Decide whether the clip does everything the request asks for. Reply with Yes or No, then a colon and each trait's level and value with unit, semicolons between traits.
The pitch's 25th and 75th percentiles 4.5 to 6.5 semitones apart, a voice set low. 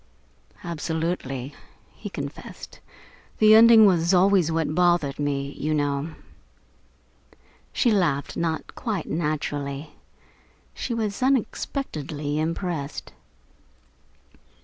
No: average, 5.1 semitones; medium, 160 Hz